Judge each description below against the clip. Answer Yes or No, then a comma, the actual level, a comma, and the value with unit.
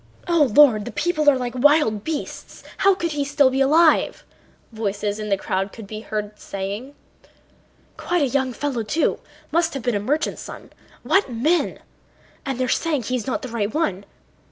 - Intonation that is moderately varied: No, wide, 5.9 semitones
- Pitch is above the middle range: Yes, very high, 260 Hz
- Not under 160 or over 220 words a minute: Yes, average, 175 wpm